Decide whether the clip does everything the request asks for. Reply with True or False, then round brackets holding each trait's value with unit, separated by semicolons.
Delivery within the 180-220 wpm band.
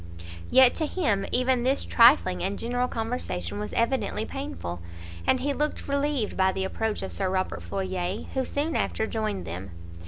False (165 wpm)